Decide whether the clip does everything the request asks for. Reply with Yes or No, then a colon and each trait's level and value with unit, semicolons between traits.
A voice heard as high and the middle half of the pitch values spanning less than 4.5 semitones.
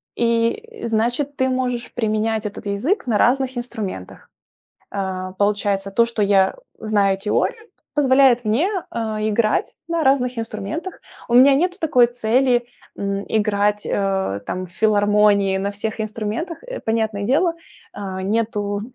Yes: high, 220 Hz; average, 4.1 semitones